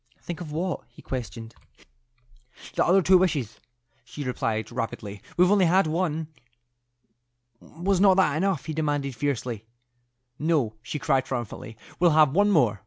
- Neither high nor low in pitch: Yes, medium, 150 Hz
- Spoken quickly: No, average, 145 wpm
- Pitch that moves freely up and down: Yes, wide, 6.6 semitones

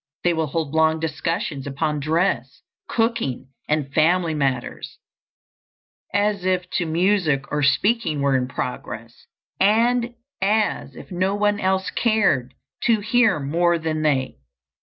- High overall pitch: No, medium, 165 Hz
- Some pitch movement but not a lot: No, wide, 6.1 semitones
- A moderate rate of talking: No, slow, 130 wpm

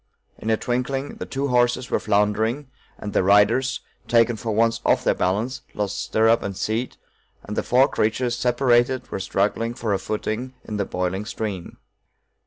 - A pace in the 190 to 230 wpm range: No, average, 170 wpm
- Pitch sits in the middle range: No, low, 115 Hz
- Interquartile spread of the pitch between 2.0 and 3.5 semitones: Yes, average, 3.0 semitones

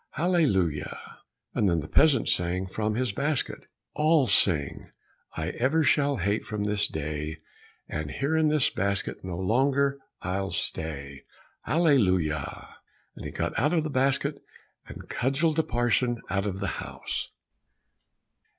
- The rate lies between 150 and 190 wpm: No, average, 140 wpm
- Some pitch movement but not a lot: No, wide, 7.6 semitones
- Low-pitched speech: Yes, low, 110 Hz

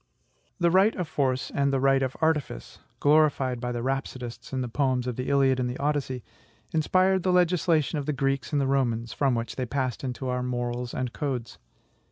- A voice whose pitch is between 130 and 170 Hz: Yes, low, 135 Hz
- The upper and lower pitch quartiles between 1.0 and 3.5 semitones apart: Yes, average, 2.9 semitones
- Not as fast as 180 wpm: No, average, 195 wpm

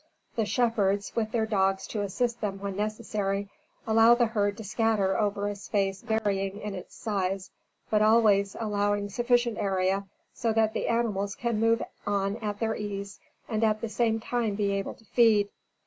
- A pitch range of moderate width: No, narrow, 2.1 semitones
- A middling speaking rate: Yes, average, 175 wpm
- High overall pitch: Yes, high, 210 Hz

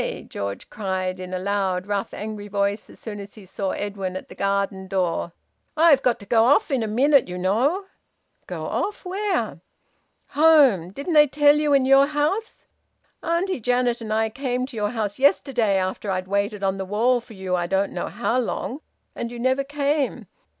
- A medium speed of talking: Yes, average, 190 wpm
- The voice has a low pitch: No, high, 220 Hz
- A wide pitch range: Yes, wide, 6.0 semitones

